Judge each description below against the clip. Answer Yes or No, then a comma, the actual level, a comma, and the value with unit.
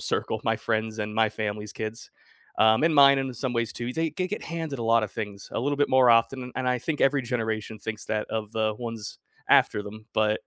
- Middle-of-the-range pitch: No, low, 115 Hz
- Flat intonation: No, average, 3.3 semitones